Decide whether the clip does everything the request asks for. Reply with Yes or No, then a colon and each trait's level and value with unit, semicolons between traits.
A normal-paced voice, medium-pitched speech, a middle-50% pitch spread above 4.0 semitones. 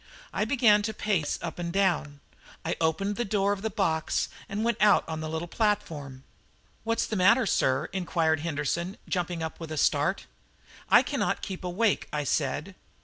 Yes: average, 175 wpm; medium, 180 Hz; average, 4.6 semitones